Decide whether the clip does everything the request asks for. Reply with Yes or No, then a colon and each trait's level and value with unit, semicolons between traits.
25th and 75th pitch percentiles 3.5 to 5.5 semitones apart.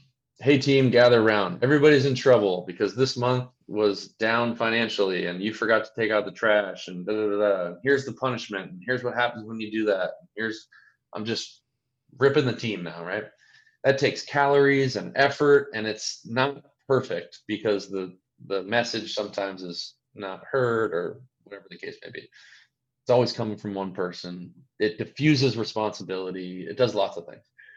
Yes: average, 4.2 semitones